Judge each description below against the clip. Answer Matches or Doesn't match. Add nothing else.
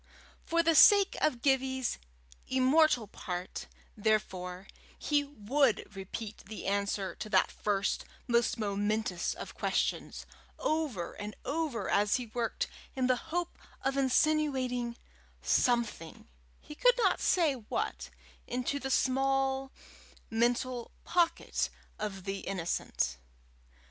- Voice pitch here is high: Matches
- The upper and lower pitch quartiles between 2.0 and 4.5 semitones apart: Doesn't match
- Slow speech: Matches